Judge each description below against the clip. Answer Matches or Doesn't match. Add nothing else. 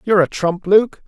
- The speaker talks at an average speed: Doesn't match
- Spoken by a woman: Doesn't match